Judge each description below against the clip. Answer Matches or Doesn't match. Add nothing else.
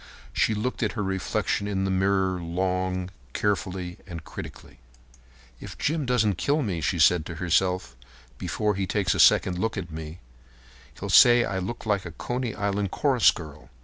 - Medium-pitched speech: Doesn't match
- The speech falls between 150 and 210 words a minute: Matches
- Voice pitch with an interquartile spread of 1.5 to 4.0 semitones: Matches